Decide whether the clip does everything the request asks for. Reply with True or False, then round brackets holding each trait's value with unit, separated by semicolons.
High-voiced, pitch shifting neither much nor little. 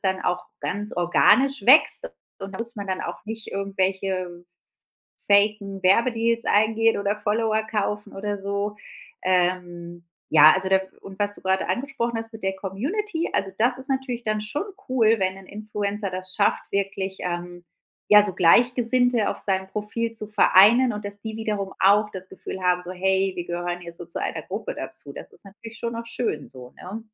True (200 Hz; 3.1 semitones)